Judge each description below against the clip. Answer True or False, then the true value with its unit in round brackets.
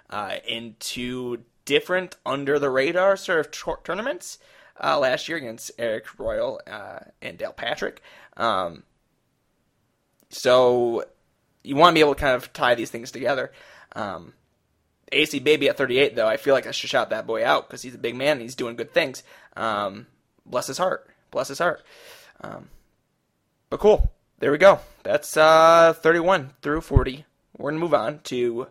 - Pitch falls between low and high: True (150 Hz)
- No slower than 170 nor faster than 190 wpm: True (175 wpm)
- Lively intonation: False (4.8 semitones)